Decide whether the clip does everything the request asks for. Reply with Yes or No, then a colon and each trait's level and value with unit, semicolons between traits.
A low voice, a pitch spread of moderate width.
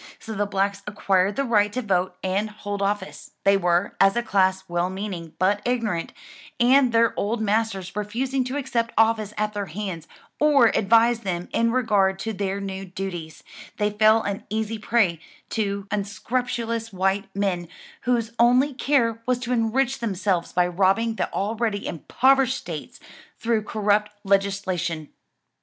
No: high, 210 Hz; average, 3.1 semitones